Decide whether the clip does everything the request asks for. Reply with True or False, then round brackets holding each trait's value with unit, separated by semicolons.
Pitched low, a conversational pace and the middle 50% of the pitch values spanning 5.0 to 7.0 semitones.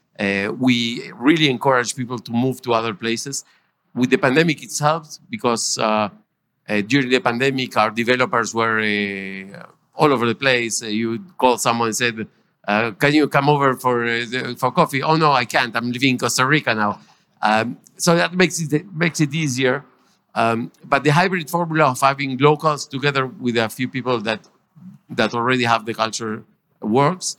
False (125 Hz; 180 wpm; 4.1 semitones)